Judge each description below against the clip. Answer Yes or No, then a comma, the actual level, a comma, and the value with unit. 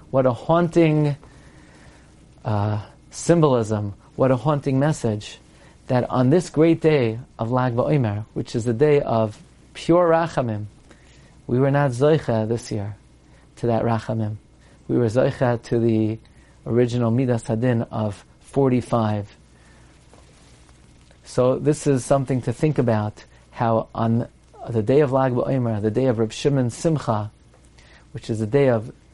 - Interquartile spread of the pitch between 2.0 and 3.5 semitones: No, average, 4.0 semitones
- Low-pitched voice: Yes, low, 120 Hz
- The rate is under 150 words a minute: Yes, average, 140 wpm